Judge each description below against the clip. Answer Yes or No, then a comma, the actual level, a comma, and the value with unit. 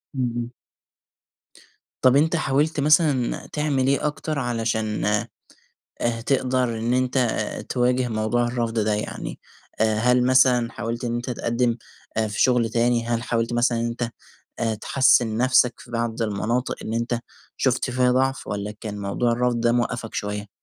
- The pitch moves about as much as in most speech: No, narrow, 1.8 semitones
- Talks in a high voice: No, low, 120 Hz